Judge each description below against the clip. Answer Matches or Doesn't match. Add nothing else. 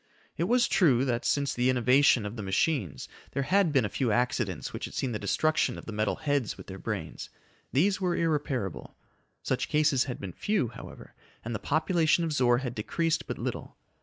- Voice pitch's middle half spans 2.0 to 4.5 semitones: Doesn't match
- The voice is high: Doesn't match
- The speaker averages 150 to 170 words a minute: Doesn't match